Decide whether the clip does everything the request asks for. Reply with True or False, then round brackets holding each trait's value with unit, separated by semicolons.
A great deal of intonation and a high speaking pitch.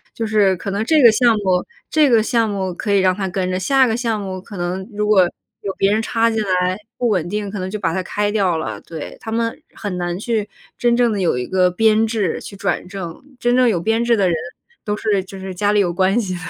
False (3.2 semitones; 205 Hz)